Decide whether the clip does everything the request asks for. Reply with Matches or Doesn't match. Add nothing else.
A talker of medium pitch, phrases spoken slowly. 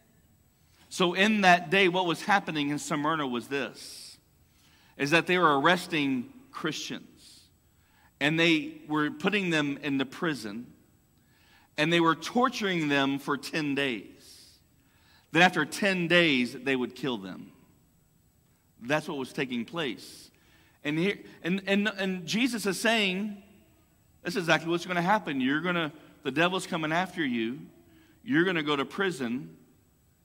Doesn't match